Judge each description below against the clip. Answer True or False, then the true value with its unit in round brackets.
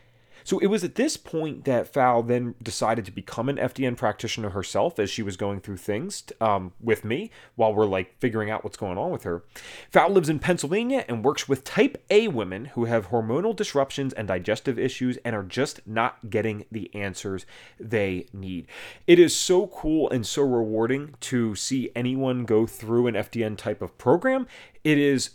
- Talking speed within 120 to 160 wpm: False (190 wpm)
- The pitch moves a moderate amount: True (4.5 semitones)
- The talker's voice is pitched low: True (120 Hz)